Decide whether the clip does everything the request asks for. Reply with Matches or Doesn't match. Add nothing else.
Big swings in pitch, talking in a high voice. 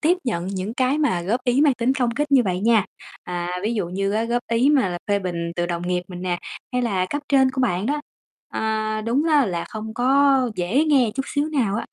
Matches